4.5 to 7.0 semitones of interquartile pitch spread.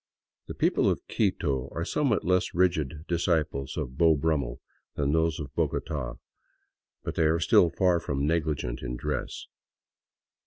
No: average, 3.4 semitones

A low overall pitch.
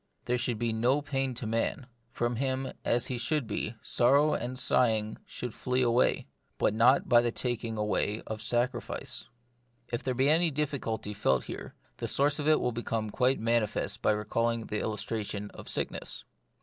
Yes: low, 120 Hz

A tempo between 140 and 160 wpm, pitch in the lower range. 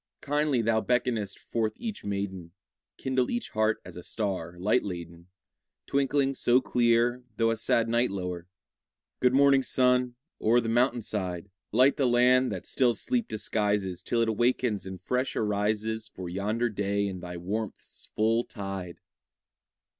Yes: average, 150 wpm; low, 110 Hz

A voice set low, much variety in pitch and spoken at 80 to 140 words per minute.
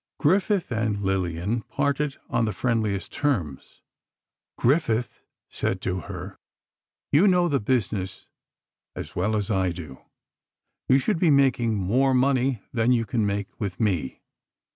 Yes: low, 115 Hz; wide, 5.8 semitones; slow, 135 wpm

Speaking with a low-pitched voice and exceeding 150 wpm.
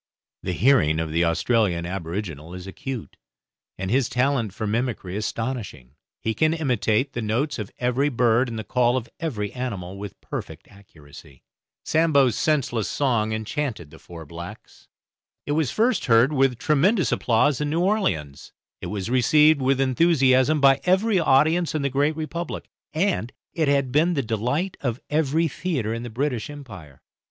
Yes: low, 125 Hz; average, 160 wpm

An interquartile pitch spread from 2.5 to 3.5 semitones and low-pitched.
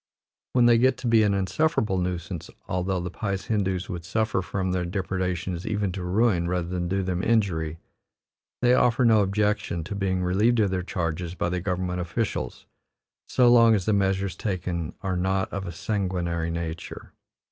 Yes: average, 2.9 semitones; very low, 95 Hz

